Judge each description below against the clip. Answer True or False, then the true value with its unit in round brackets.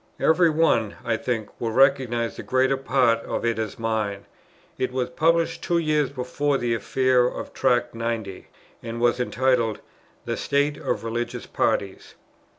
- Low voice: True (125 Hz)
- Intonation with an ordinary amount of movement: True (3.0 semitones)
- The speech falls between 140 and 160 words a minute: True (155 wpm)